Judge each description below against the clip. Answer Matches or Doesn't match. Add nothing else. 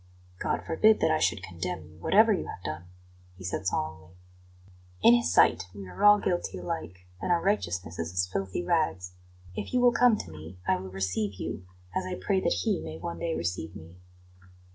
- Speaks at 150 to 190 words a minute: Doesn't match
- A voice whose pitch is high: Doesn't match